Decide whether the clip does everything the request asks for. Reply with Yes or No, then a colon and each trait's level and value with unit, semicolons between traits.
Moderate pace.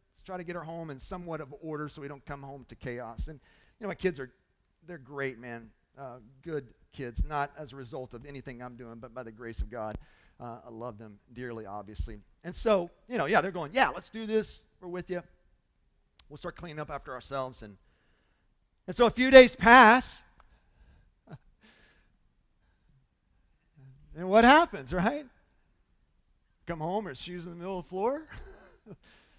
Yes: average, 180 wpm